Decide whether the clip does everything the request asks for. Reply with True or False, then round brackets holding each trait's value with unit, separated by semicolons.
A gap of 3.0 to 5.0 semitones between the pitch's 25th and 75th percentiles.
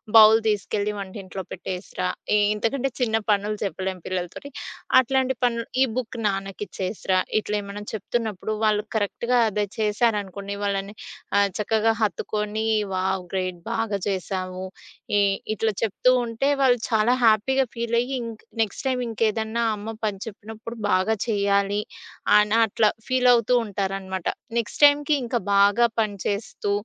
False (2.6 semitones)